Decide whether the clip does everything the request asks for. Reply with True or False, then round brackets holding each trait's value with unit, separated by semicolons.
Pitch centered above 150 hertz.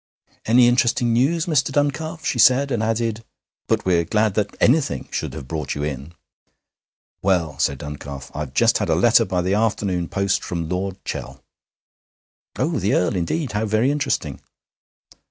False (105 Hz)